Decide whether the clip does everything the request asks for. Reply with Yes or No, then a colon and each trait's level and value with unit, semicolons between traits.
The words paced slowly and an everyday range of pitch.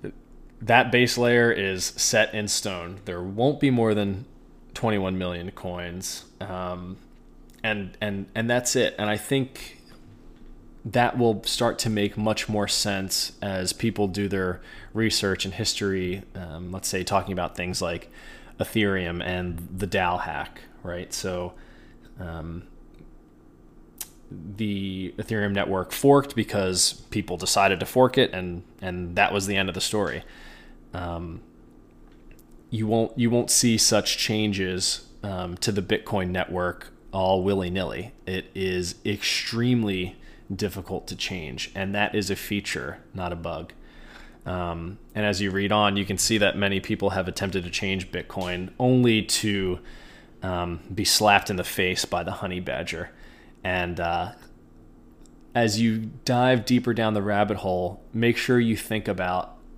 No: average, 150 wpm; average, 3.0 semitones